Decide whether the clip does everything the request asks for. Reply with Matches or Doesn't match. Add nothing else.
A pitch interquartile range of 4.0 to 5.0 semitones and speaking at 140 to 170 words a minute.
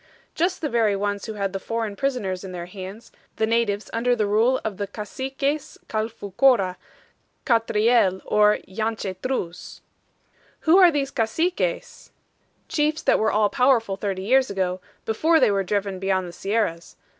Matches